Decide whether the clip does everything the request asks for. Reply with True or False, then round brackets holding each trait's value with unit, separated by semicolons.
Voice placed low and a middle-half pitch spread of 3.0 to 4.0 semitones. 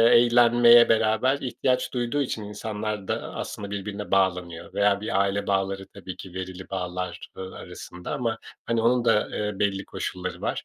True (105 Hz; 3.4 semitones)